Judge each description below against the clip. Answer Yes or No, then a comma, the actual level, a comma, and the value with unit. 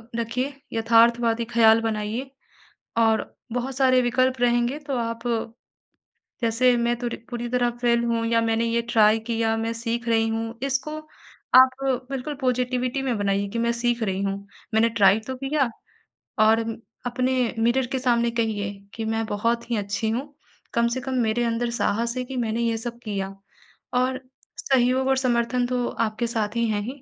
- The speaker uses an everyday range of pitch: No, narrow, 2.0 semitones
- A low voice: No, high, 235 Hz